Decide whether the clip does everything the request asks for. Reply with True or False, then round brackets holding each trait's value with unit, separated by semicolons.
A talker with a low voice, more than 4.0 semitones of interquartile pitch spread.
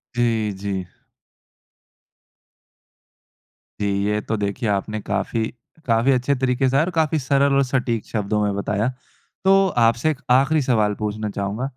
True (115 Hz; 4.4 semitones)